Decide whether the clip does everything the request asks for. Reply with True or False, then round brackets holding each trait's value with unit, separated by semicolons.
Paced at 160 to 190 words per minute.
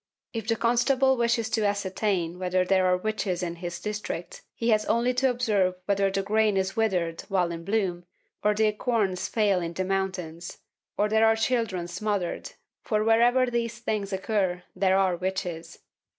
True (170 wpm)